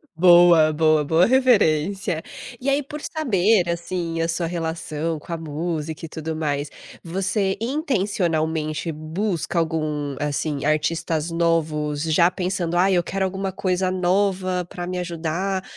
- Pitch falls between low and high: Yes, medium, 170 Hz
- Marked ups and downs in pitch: No, average, 3.0 semitones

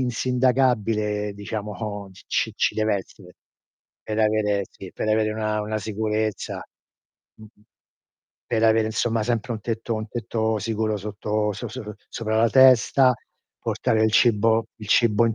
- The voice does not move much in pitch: Yes, narrow, 1.3 semitones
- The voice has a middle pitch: No, low, 110 Hz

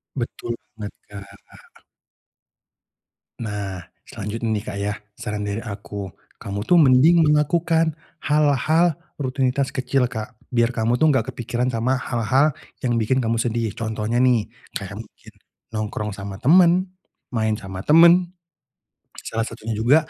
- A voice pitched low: Yes, low, 120 Hz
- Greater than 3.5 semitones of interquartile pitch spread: Yes, average, 4.6 semitones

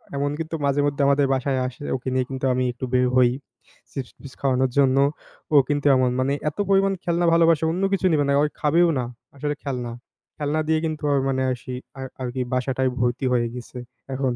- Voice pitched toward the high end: No, low, 135 Hz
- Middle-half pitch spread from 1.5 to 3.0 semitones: Yes, narrow, 2.6 semitones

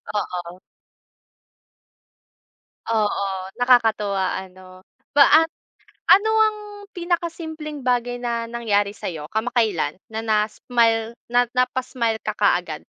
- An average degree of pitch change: Yes, average, 3.7 semitones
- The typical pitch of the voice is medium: No, high, 230 Hz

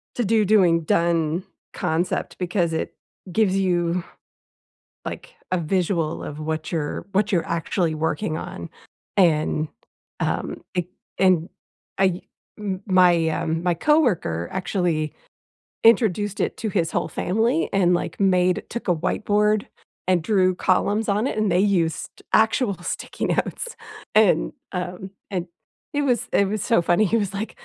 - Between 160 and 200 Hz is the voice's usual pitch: Yes, medium, 185 Hz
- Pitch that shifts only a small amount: No, average, 3.7 semitones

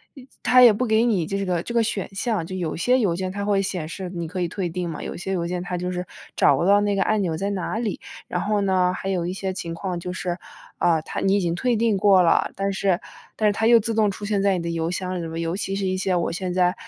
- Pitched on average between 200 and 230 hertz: No, high, 190 Hz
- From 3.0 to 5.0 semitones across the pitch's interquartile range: No, narrow, 2.4 semitones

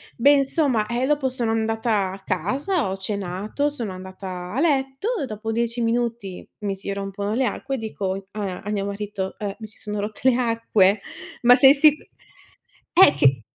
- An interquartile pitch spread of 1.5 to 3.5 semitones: No, average, 4.8 semitones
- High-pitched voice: Yes, high, 220 Hz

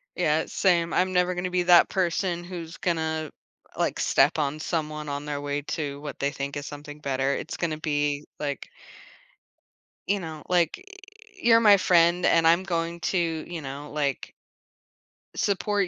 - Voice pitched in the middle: Yes, medium, 165 Hz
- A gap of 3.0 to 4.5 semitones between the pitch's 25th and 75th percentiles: Yes, average, 3.5 semitones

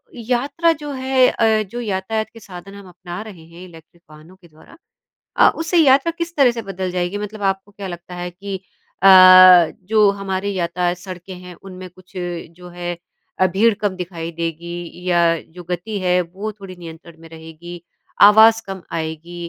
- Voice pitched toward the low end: No, medium, 185 Hz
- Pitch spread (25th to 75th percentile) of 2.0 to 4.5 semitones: Yes, average, 3.7 semitones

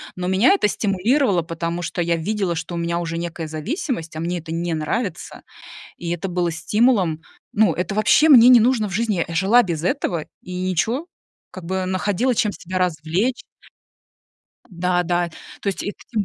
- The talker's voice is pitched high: No, medium, 180 Hz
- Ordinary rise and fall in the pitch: Yes, average, 4.2 semitones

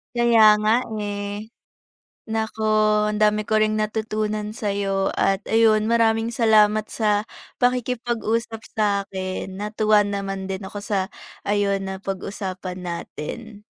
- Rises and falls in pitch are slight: Yes, narrow, 1.7 semitones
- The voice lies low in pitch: No, high, 210 Hz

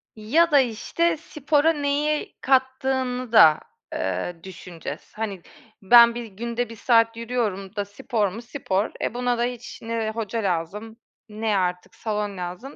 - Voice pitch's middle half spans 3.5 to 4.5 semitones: Yes, average, 4.0 semitones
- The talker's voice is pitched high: Yes, high, 230 Hz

